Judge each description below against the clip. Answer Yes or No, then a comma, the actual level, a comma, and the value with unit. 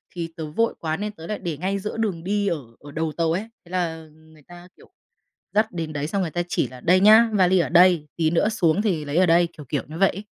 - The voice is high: No, medium, 175 Hz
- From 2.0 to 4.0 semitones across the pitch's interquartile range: Yes, average, 3.6 semitones